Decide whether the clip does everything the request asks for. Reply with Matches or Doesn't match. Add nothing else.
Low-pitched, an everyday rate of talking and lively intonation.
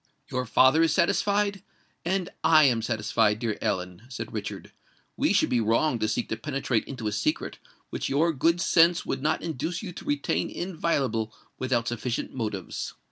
Matches